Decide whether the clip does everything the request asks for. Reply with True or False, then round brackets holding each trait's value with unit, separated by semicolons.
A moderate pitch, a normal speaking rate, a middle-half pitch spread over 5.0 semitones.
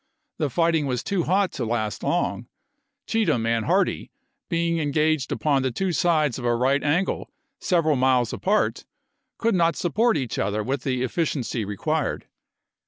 True (145 Hz; 160 wpm; 5.5 semitones)